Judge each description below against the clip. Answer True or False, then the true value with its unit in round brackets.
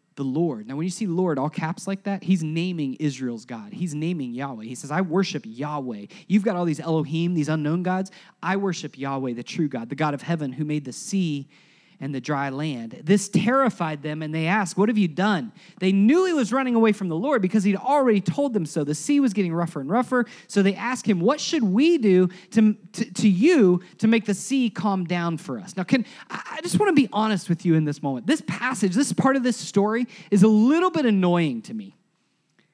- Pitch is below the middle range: False (185 Hz)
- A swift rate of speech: True (235 wpm)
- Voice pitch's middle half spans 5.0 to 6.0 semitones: True (5.5 semitones)